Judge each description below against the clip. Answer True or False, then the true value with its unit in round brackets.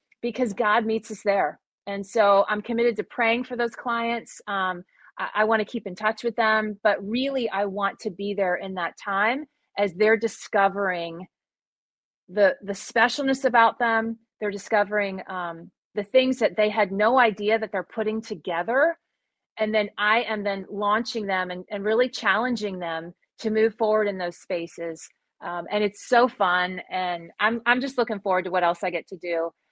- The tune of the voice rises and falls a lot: False (3.1 semitones)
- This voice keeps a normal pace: True (185 wpm)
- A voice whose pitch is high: True (210 Hz)